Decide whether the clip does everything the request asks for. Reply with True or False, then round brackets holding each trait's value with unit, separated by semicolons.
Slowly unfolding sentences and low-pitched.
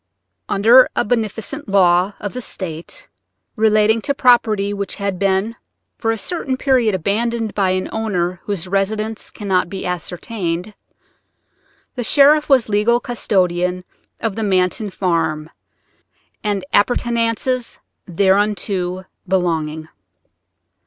False (110 wpm; 205 Hz)